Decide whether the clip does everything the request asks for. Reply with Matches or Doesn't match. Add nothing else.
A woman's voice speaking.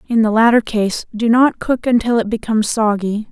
Matches